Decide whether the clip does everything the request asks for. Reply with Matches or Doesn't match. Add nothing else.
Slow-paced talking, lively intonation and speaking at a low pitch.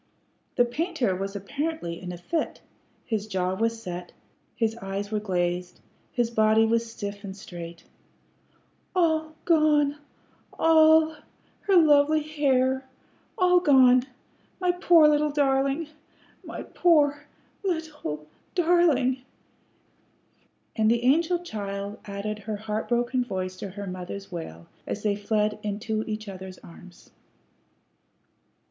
Doesn't match